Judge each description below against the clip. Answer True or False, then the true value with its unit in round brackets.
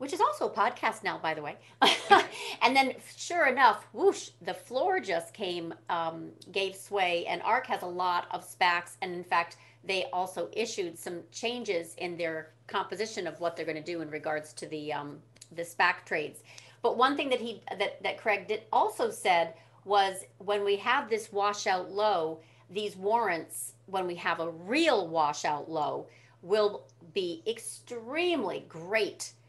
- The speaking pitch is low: False (190 Hz)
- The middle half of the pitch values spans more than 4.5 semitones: True (5.3 semitones)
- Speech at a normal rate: True (170 wpm)